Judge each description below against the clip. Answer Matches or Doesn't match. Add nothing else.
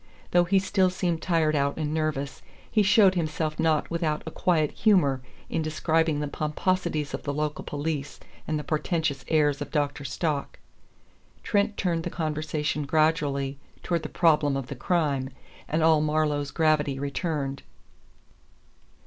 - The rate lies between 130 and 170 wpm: Matches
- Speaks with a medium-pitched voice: Matches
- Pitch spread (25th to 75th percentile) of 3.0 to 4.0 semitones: Doesn't match